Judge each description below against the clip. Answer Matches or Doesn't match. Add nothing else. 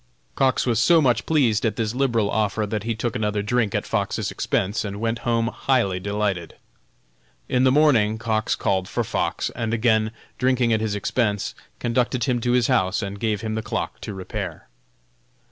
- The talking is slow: Doesn't match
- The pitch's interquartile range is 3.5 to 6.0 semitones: Doesn't match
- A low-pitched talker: Matches